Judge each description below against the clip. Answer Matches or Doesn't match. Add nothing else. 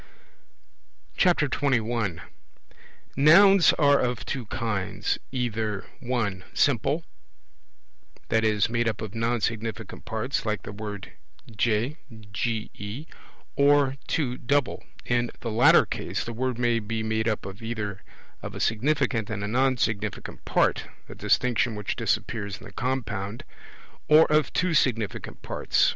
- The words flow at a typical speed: Doesn't match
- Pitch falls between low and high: Doesn't match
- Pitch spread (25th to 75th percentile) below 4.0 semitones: Matches